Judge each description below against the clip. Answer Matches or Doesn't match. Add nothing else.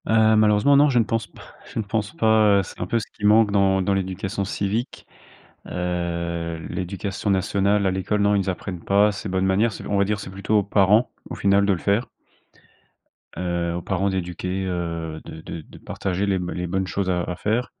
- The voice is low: Matches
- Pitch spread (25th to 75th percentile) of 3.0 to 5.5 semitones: Doesn't match